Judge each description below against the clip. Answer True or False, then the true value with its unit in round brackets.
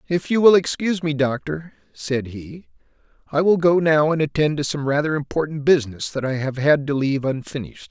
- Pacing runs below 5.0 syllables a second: False (5.6 syllables/s)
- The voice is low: False (145 Hz)